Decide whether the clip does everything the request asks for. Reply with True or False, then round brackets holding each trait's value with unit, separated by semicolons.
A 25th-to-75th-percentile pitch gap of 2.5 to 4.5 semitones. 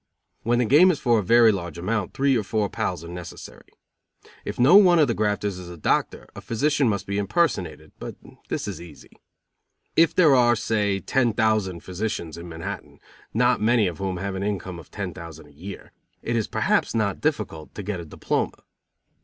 False (4.9 semitones)